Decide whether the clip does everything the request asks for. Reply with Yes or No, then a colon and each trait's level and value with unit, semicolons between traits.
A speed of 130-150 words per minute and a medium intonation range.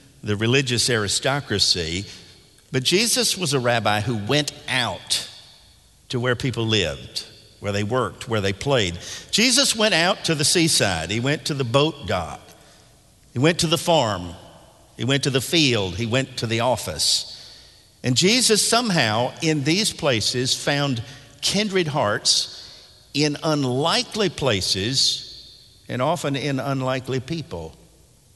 No: average, 140 wpm; wide, 5.9 semitones